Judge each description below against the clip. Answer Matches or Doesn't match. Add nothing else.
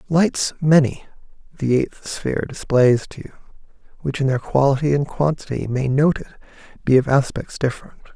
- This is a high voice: Doesn't match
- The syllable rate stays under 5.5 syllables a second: Matches